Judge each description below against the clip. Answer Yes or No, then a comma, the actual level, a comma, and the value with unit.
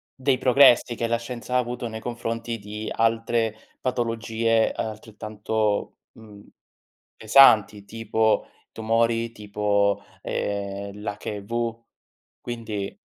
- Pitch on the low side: Yes, low, 115 Hz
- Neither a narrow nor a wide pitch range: No, narrow, 1.9 semitones